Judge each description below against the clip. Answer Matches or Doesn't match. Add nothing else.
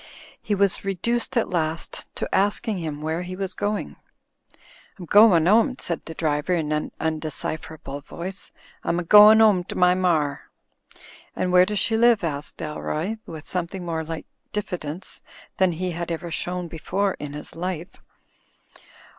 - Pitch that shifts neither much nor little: Matches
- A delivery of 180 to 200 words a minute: Doesn't match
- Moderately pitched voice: Matches